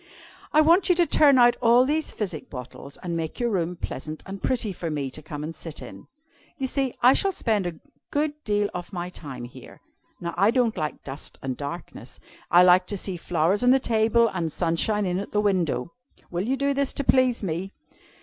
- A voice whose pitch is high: Yes, high, 195 Hz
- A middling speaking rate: No, fast, 210 wpm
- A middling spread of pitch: No, wide, 7.0 semitones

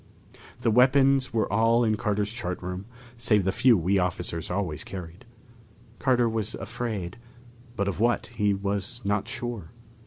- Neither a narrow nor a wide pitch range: Yes, average, 3.8 semitones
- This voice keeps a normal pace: Yes, average, 150 wpm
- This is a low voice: Yes, low, 105 Hz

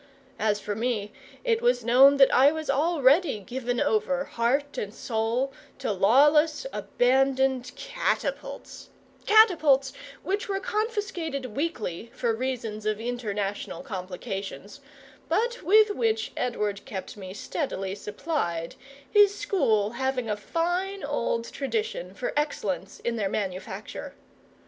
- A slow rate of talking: Yes, slow, 120 wpm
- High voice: Yes, very high, 255 Hz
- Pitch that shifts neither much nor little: No, wide, 6.9 semitones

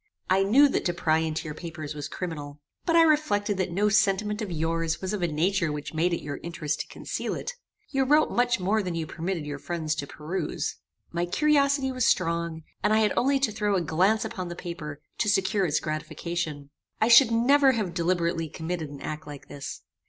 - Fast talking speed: Yes, fast, 210 wpm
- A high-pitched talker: No, medium, 175 Hz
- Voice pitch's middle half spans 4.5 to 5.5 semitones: Yes, average, 5.1 semitones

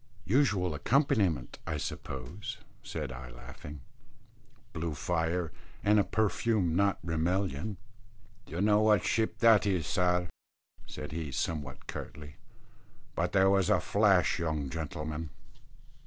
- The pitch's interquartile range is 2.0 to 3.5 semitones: No, average, 4.7 semitones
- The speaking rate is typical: No, slow, 115 wpm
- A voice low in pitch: Yes, very low, 90 Hz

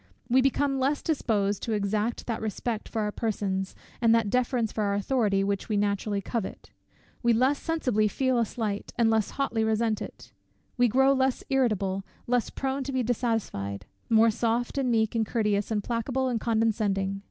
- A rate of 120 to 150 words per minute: No, average, 175 wpm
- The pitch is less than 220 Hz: No, high, 225 Hz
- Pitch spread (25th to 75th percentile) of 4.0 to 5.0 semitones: No, average, 3.3 semitones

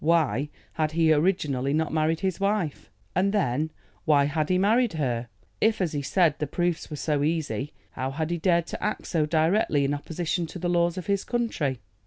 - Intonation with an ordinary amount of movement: Yes, average, 3.5 semitones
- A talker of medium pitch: Yes, medium, 160 Hz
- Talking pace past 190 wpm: Yes, average, 200 wpm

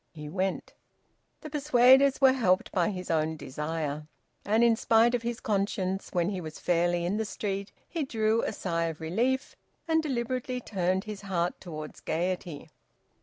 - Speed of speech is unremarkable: Yes, average, 165 wpm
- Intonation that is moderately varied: No, wide, 5.7 semitones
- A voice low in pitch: No, high, 195 Hz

